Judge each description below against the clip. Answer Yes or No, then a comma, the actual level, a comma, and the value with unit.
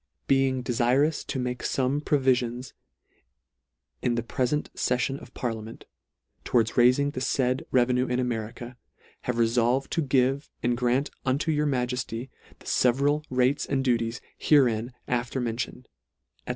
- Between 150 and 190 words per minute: No, average, 140 wpm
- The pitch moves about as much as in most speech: No, narrow, 1.9 semitones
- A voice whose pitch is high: No, low, 125 Hz